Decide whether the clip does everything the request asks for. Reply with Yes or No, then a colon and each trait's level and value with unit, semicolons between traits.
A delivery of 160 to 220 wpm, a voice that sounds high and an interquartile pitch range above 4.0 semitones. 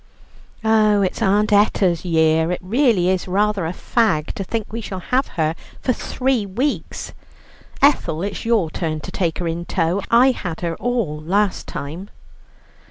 Yes: average, 165 wpm; high, 195 Hz; average, 4.9 semitones